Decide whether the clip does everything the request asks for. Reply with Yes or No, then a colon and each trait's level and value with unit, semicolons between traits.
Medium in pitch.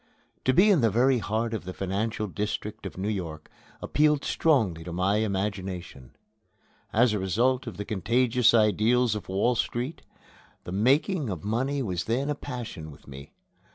No: low, 110 Hz